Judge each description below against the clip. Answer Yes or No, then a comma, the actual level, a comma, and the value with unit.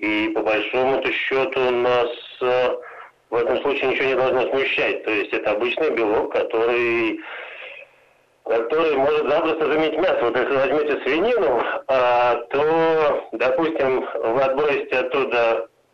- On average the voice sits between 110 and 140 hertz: Yes, low, 135 Hz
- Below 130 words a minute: No, average, 135 wpm